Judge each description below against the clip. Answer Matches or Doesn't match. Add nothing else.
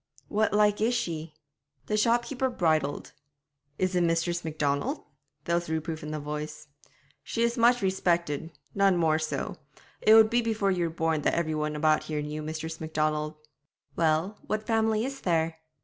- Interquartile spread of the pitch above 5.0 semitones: Matches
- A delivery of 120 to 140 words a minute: Doesn't match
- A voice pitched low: Doesn't match